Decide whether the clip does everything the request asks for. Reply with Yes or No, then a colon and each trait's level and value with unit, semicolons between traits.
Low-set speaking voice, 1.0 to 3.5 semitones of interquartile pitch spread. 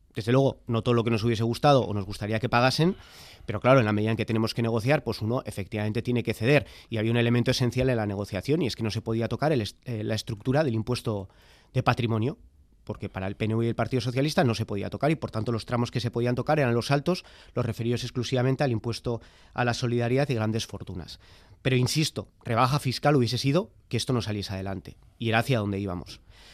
Yes: low, 115 Hz; average, 3.0 semitones